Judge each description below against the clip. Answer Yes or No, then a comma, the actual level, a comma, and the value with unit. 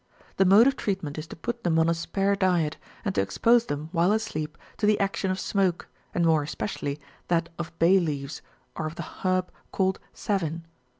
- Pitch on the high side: No, medium, 175 Hz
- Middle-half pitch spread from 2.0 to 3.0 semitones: No, average, 3.5 semitones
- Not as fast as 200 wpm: No, fast, 205 wpm